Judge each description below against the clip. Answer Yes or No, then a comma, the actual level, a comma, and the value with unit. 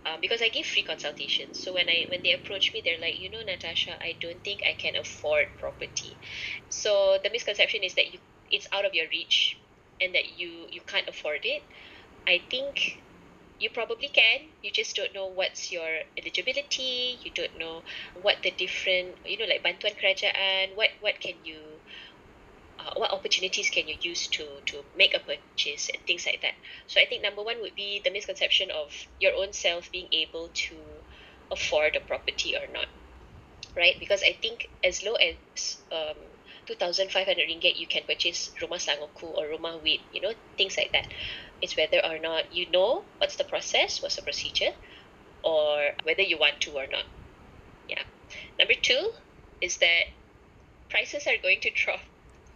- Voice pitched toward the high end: Yes, high, 200 Hz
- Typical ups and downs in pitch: No, wide, 9.0 semitones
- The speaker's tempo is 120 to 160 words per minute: No, average, 185 wpm